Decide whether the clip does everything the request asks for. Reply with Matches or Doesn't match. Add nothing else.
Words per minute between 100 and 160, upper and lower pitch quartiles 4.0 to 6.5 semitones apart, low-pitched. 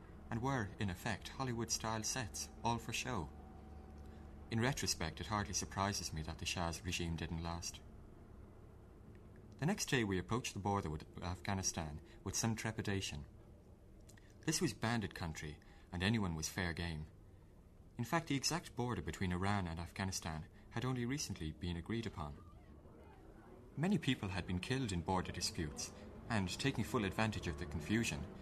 Matches